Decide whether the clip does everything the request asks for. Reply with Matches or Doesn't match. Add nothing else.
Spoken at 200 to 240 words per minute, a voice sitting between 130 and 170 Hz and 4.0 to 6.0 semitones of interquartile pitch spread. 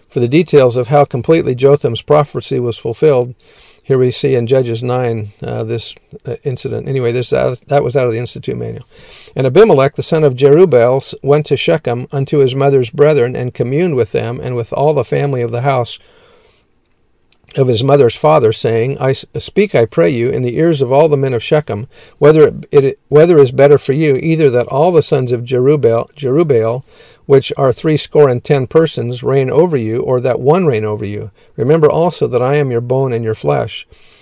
Doesn't match